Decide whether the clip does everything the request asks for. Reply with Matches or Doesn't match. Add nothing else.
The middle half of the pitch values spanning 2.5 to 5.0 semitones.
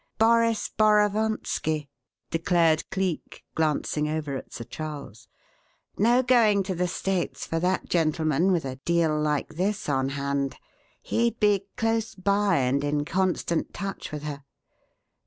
Doesn't match